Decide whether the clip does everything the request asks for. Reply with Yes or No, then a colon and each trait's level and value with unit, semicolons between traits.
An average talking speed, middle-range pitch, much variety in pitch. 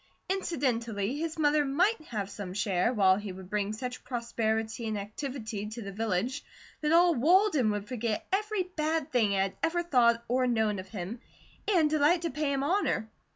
No: average, 180 wpm; high, 240 Hz; wide, 6.5 semitones